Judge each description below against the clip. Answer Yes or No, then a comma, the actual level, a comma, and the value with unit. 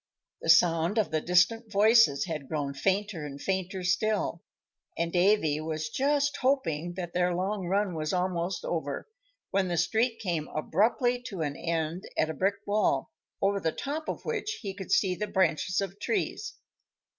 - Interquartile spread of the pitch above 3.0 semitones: Yes, average, 4.3 semitones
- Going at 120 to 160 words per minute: No, average, 170 wpm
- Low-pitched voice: No, medium, 185 Hz